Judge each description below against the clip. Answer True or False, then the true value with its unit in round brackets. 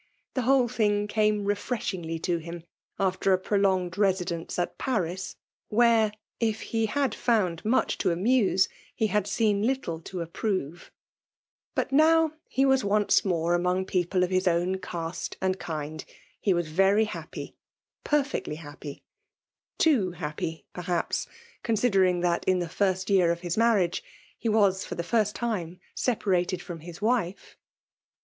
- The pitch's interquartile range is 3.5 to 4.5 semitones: True (4.0 semitones)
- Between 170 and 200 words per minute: False (155 wpm)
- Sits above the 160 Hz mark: True (190 Hz)